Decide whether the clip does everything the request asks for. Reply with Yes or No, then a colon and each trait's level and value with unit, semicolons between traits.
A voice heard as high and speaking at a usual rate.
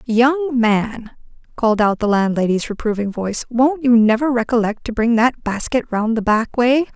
Yes: high, 235 Hz; average, 175 wpm